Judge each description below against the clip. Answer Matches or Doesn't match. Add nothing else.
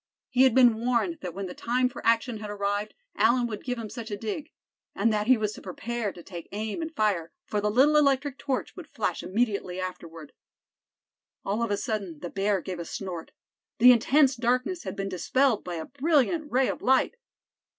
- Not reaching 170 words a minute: Doesn't match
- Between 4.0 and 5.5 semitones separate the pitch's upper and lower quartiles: Matches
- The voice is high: Matches